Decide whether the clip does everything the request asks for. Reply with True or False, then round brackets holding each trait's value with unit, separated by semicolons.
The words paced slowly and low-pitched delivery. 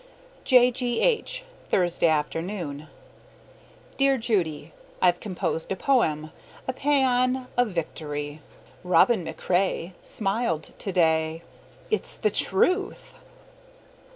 False (95 wpm; 190 Hz)